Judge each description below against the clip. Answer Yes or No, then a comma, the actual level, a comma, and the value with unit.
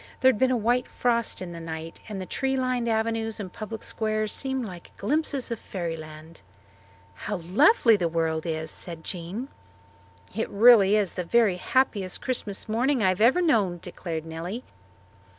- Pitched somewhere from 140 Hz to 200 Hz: No, high, 210 Hz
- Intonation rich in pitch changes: Yes, wide, 5.7 semitones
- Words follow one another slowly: No, average, 170 wpm